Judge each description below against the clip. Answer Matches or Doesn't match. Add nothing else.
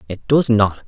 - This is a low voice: Matches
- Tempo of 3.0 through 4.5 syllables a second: Matches